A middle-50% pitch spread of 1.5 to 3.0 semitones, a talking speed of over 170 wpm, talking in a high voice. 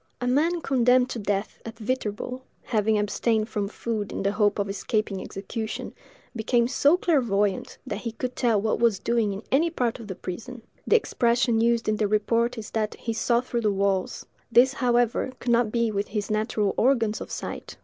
Yes: average, 2.7 semitones; average, 190 wpm; high, 225 Hz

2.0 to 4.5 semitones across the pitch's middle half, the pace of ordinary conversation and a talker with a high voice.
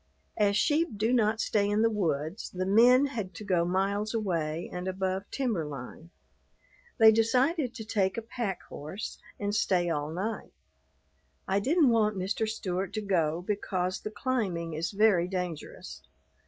Yes: average, 3.7 semitones; average, 155 wpm; high, 200 Hz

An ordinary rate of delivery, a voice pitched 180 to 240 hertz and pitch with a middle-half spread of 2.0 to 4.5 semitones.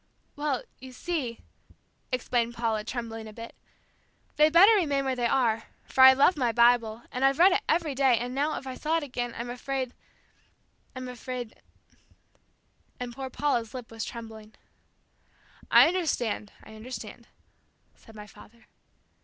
No: average, 155 wpm; very high, 250 Hz; average, 3.0 semitones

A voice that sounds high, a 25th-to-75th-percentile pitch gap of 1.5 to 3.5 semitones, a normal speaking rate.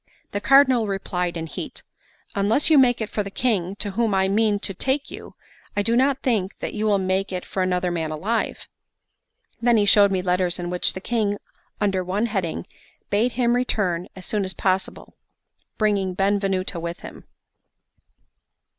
Yes: high, 200 Hz; average, 3.2 semitones; average, 175 wpm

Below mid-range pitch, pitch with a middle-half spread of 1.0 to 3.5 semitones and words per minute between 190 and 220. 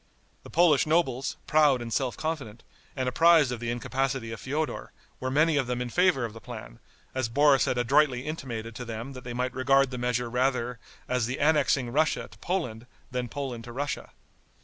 Yes: low, 130 Hz; average, 3.1 semitones; average, 195 wpm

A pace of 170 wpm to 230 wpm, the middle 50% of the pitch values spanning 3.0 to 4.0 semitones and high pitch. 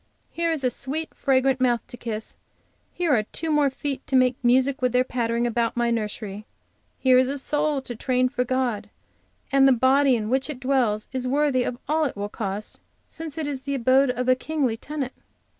No: average, 200 wpm; narrow, 2.6 semitones; very high, 255 Hz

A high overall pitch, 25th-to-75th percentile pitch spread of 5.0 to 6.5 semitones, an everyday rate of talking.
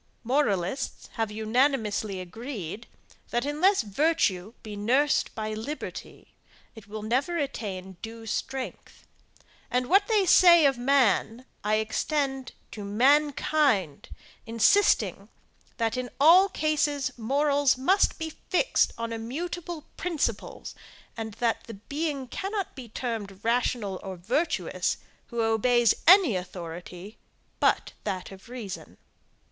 No: high, 245 Hz; wide, 5.4 semitones; slow, 115 wpm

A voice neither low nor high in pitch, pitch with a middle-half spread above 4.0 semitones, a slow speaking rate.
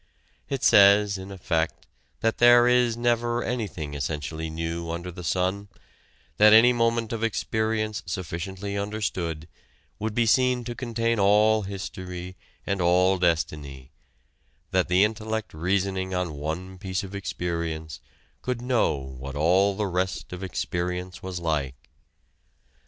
No: very low, 95 Hz; average, 4.5 semitones; slow, 130 wpm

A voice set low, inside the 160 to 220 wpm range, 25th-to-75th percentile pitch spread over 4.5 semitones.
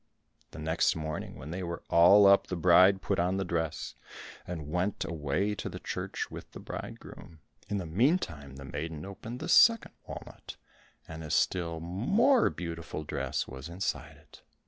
No: very low, 85 Hz; average, 170 wpm; average, 3.7 semitones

